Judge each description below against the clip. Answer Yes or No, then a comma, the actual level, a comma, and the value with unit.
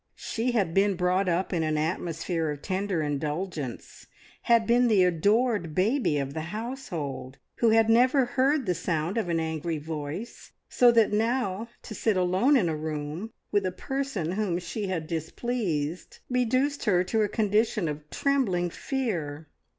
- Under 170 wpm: Yes, average, 160 wpm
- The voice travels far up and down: Yes, wide, 6.0 semitones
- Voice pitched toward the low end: No, medium, 185 Hz